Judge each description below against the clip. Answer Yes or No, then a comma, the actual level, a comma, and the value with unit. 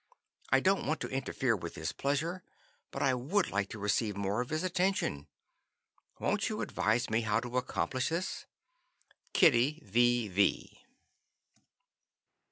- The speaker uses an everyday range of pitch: No, wide, 6.6 semitones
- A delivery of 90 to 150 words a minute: Yes, average, 140 wpm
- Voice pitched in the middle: No, low, 125 Hz